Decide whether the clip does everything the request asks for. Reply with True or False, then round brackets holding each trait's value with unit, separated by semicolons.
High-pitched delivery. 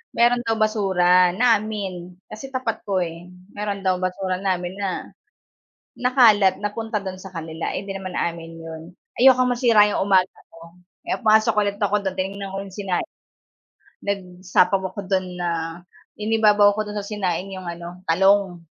True (195 Hz)